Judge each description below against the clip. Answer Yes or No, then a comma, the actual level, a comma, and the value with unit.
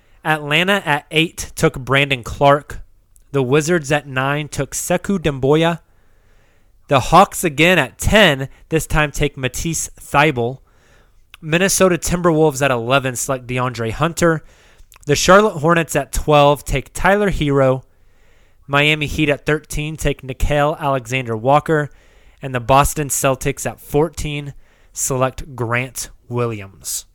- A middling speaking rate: No, slow, 120 wpm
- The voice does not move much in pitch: No, average, 4.0 semitones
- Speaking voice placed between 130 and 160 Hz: Yes, medium, 140 Hz